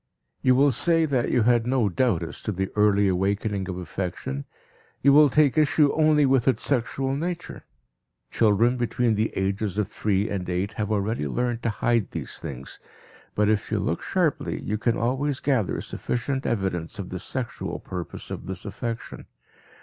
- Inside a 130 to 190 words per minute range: Yes, average, 175 wpm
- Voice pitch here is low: Yes, low, 110 Hz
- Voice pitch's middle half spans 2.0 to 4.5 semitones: No, average, 5.1 semitones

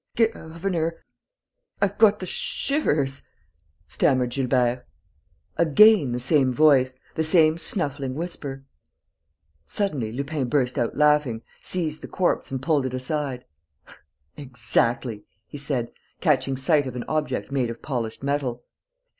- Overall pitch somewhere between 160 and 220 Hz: No, medium, 140 Hz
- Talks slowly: Yes, slow, 120 wpm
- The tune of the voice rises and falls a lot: No, average, 3.8 semitones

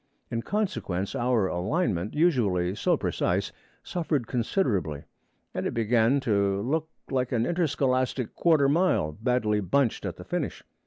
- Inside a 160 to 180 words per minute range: No, slow, 135 wpm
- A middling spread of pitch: No, wide, 6.4 semitones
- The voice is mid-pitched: No, low, 120 Hz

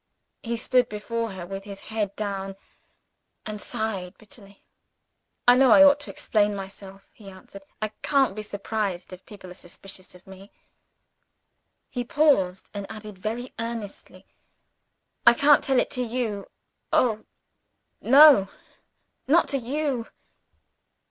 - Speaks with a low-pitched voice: No, high, 215 Hz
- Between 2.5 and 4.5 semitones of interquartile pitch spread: Yes, average, 4.0 semitones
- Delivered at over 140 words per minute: No, slow, 135 wpm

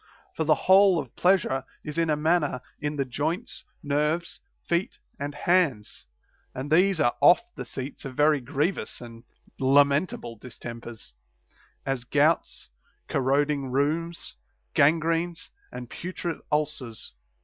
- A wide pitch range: No, average, 3.9 semitones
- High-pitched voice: No, medium, 150 Hz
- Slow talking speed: Yes, slow, 125 wpm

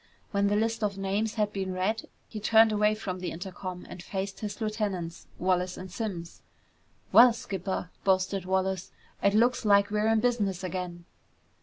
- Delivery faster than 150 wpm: Yes, average, 165 wpm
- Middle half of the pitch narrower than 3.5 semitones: Yes, narrow, 2.5 semitones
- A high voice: Yes, high, 200 Hz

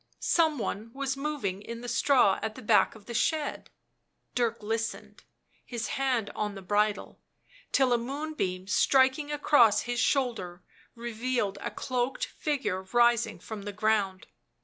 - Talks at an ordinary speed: Yes, average, 145 wpm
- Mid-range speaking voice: No, high, 235 Hz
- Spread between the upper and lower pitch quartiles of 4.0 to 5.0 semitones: Yes, average, 4.3 semitones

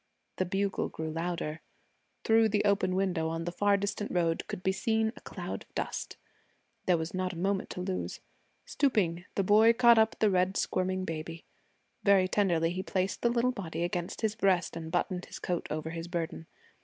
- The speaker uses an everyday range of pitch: Yes, average, 3.2 semitones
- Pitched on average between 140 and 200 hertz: Yes, medium, 185 Hz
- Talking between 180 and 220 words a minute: Yes, average, 190 wpm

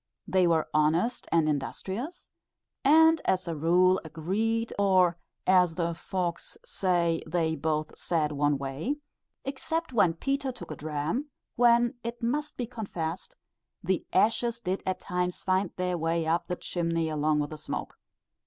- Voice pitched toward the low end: No, medium, 180 Hz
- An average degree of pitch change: No, wide, 6.2 semitones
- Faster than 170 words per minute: No, average, 150 wpm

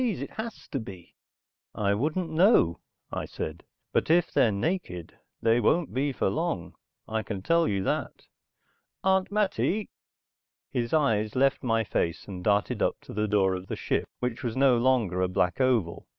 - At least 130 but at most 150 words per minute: No, average, 175 wpm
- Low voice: Yes, low, 120 Hz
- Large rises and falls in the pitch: Yes, wide, 8.1 semitones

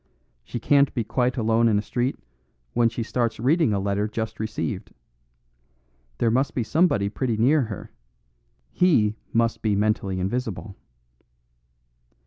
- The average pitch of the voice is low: Yes, low, 115 Hz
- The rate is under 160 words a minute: Yes, slow, 135 wpm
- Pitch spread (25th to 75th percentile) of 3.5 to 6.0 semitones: No, average, 3.0 semitones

